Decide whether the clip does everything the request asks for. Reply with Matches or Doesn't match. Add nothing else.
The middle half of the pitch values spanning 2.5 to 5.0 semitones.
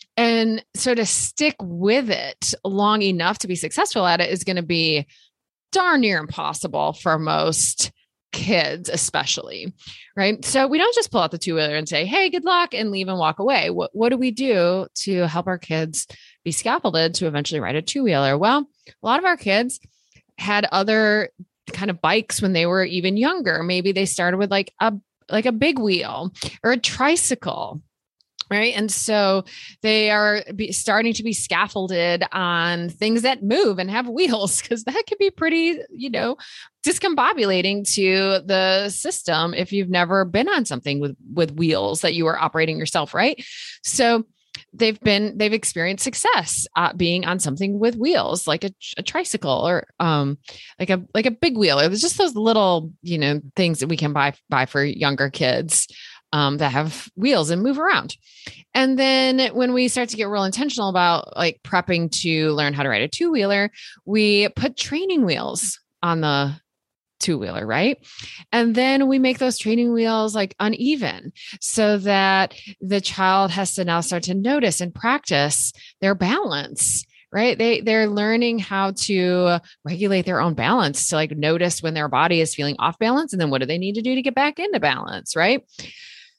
Doesn't match